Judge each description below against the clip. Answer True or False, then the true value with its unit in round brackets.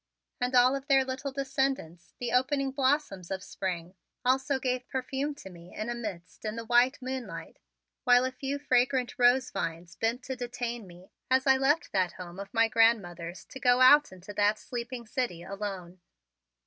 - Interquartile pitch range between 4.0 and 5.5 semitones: True (5.2 semitones)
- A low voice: False (245 Hz)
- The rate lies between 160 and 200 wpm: True (175 wpm)